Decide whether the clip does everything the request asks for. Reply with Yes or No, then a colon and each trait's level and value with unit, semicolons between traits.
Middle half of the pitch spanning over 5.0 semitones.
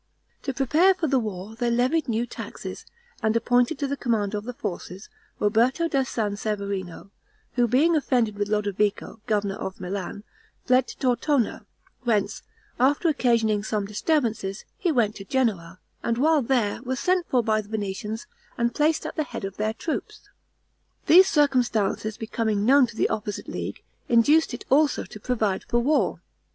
No: average, 4.4 semitones